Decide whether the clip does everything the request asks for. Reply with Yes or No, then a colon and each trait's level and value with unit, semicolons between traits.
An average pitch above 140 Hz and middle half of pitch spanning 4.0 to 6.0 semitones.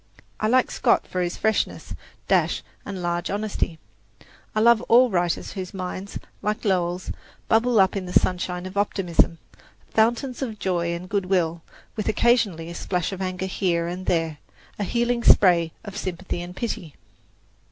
No: medium, 185 Hz; average, 3.6 semitones